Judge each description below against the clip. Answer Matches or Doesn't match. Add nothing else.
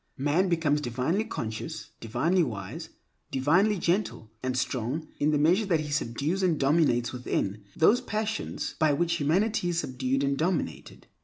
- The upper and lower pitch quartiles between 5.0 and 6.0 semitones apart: Matches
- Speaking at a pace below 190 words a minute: Matches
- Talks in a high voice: Doesn't match